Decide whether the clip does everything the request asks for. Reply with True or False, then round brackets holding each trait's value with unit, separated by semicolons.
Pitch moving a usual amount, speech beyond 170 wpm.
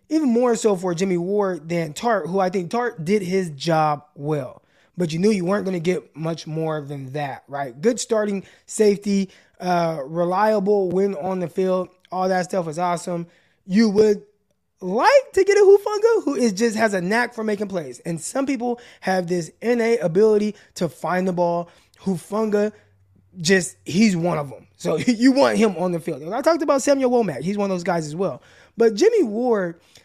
True (4.5 semitones; 200 wpm)